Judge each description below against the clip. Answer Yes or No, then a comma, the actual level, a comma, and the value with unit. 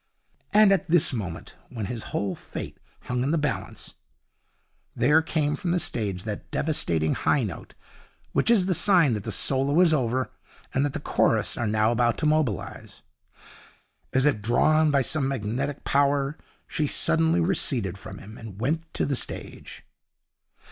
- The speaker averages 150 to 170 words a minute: Yes, average, 165 wpm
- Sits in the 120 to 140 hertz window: Yes, low, 135 Hz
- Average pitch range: No, wide, 5.9 semitones